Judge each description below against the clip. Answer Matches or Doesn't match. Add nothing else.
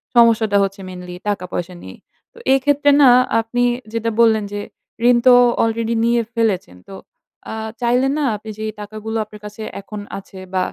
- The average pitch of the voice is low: Doesn't match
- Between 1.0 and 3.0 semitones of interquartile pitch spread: Matches